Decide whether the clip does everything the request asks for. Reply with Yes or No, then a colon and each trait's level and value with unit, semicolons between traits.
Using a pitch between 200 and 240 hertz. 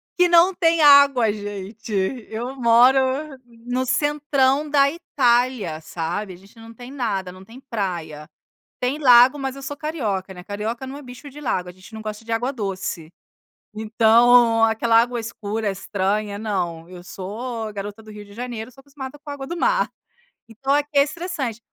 Yes: high, 230 Hz